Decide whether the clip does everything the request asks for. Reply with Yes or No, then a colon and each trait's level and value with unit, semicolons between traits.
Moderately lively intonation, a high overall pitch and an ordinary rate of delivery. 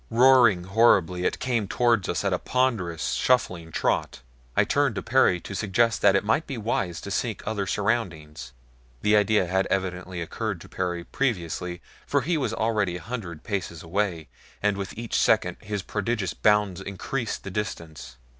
No: average, 4.3 semitones; low, 100 Hz; average, 170 wpm